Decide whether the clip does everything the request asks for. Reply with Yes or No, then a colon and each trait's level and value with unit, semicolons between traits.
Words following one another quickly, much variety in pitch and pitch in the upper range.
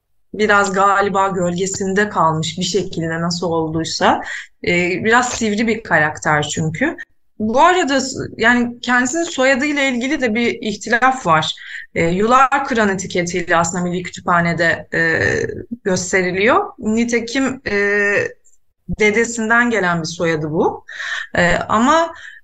No: average, 110 wpm; wide, 6.3 semitones; high, 210 Hz